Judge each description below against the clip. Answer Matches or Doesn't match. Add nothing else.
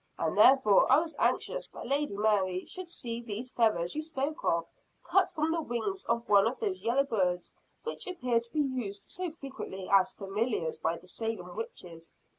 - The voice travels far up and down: Matches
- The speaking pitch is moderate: Doesn't match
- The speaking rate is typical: Matches